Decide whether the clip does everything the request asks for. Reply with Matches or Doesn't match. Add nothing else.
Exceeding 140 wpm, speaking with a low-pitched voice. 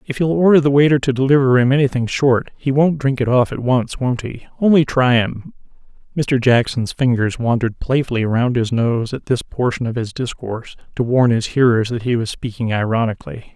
Matches